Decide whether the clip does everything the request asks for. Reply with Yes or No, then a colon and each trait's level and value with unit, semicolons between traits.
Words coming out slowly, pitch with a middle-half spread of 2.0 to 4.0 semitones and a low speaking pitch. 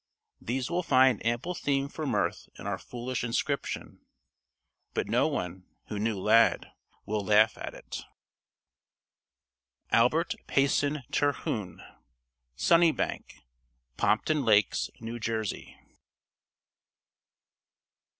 No: slow, 95 wpm; average, 4.7 semitones; low, 120 Hz